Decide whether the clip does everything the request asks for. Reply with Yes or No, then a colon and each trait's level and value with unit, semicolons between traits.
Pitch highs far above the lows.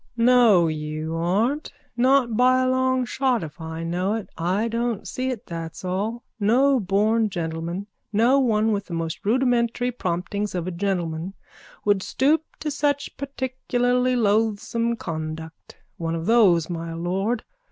Yes: wide, 6.4 semitones